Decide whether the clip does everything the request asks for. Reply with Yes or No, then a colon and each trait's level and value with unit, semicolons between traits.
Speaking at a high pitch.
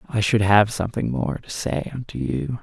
No: low, 110 Hz